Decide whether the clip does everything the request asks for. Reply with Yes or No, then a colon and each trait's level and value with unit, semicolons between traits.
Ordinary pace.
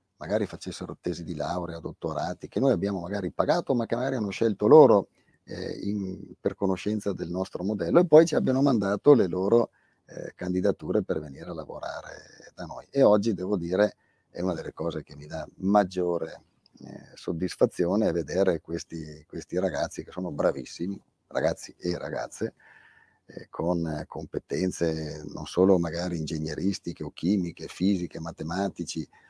Yes: average, 150 wpm